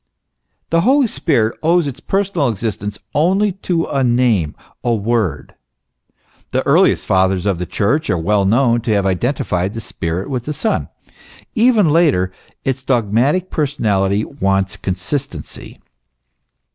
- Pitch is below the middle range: Yes, low, 120 Hz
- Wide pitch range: Yes, wide, 7.8 semitones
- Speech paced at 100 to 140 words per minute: Yes, slow, 135 wpm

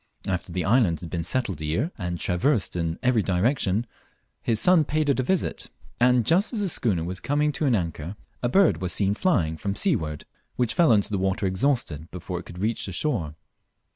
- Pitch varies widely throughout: Yes, wide, 7.3 semitones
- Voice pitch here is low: Yes, low, 100 Hz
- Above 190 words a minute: Yes, fast, 205 wpm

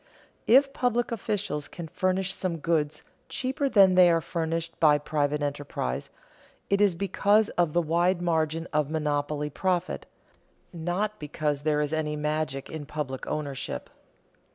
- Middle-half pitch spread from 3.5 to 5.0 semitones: Yes, average, 3.8 semitones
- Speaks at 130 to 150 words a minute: Yes, average, 140 wpm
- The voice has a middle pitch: Yes, medium, 160 Hz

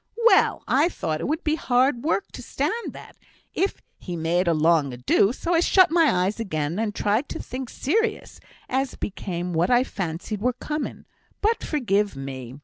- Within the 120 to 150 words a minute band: No, average, 180 wpm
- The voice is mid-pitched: No, high, 215 Hz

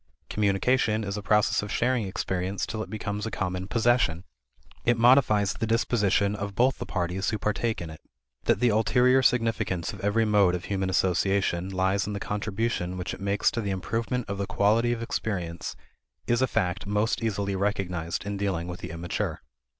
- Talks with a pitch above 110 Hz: No, low, 100 Hz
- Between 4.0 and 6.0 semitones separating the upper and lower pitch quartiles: No, average, 3.1 semitones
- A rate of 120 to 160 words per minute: No, average, 185 wpm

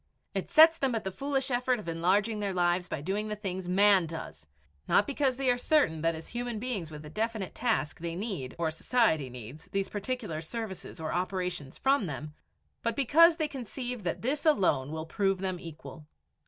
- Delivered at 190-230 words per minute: Yes, average, 195 wpm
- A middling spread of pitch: No, wide, 6.8 semitones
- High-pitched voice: Yes, high, 195 Hz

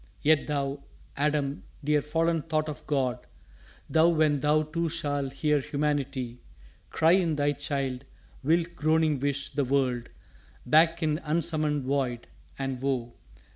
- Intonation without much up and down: Yes, narrow, 2.3 semitones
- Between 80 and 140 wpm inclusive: Yes, slow, 135 wpm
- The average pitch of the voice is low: No, medium, 145 Hz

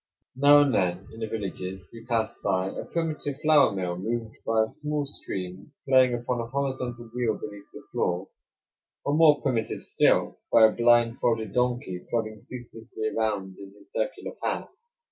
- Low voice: Yes, low, 115 Hz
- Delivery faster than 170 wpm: No, average, 165 wpm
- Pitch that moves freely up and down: No, average, 4.2 semitones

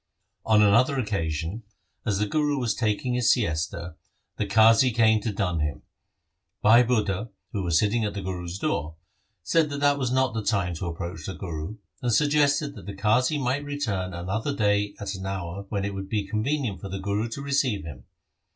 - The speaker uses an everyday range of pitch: Yes, average, 4.6 semitones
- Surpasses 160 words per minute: Yes, average, 190 wpm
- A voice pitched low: Yes, low, 105 Hz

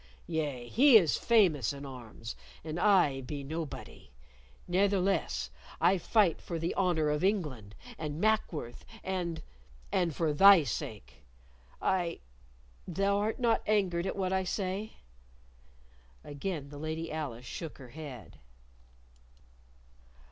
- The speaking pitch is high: No, medium, 165 Hz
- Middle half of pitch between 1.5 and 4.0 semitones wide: No, average, 5.1 semitones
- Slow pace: Yes, slow, 120 wpm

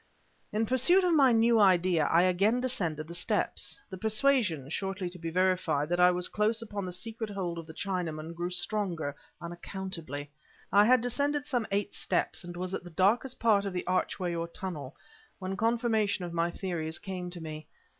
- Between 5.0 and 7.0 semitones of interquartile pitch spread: No, average, 4.2 semitones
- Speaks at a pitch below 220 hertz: Yes, medium, 185 Hz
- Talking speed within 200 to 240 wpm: No, average, 185 wpm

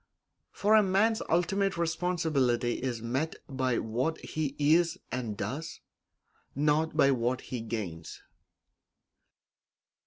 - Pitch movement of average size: No, wide, 5.8 semitones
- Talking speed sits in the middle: No, slow, 105 wpm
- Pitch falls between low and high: Yes, medium, 145 Hz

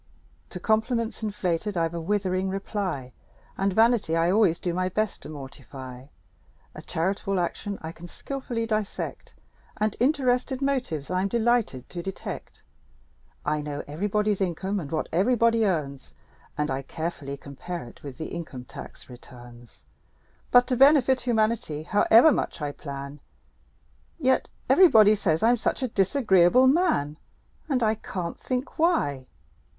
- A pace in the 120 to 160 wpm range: Yes, average, 140 wpm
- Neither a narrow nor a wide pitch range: No, wide, 6.9 semitones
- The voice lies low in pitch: No, high, 190 Hz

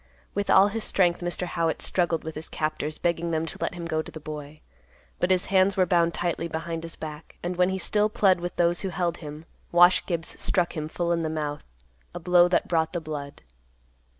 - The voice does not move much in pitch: Yes, narrow, 2.1 semitones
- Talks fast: Yes, fast, 220 wpm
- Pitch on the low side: No, medium, 170 Hz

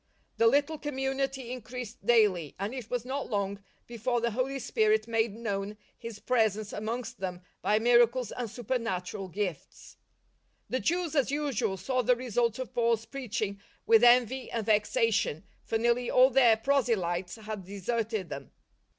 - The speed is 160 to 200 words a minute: No, average, 150 wpm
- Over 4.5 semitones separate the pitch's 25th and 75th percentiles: No, average, 3.3 semitones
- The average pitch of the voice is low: No, high, 230 Hz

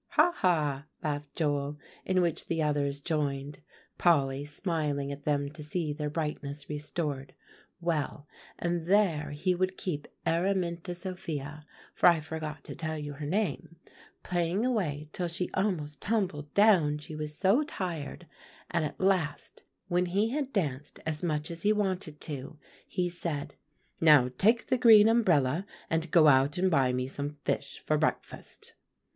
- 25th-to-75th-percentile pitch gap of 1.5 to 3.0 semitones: No, average, 3.7 semitones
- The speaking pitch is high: No, medium, 155 Hz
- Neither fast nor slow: Yes, average, 155 wpm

